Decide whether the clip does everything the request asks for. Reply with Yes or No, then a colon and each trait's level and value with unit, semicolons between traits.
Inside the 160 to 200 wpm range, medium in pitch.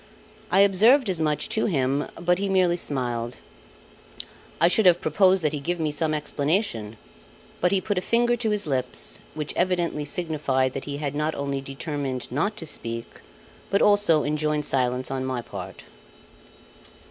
Yes: average, 165 wpm; medium, 155 Hz